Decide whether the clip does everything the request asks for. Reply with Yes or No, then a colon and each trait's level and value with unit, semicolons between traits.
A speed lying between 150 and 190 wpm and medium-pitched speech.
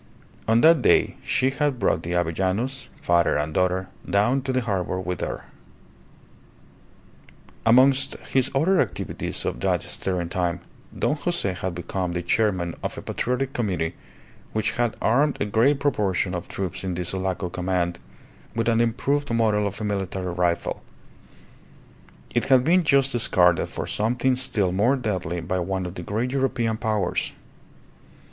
No: average, 155 wpm; low, 105 Hz